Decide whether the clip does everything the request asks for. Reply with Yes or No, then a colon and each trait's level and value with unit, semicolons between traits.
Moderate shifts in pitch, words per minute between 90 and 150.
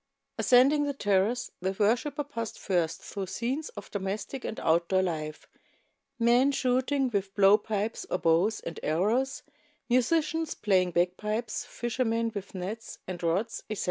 Yes: average, 4.8 semitones; average, 145 wpm